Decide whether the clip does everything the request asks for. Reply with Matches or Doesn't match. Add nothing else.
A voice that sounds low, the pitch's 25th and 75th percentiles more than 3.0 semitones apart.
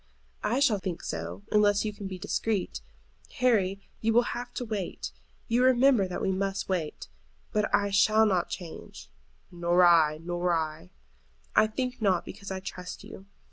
Doesn't match